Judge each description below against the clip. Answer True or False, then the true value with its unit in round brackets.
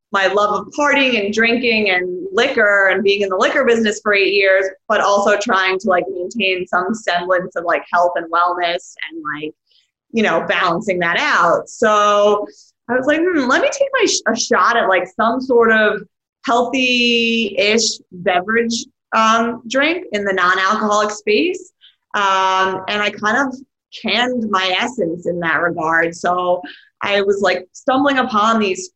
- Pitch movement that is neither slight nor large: True (4.2 semitones)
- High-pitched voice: True (205 Hz)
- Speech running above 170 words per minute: False (165 wpm)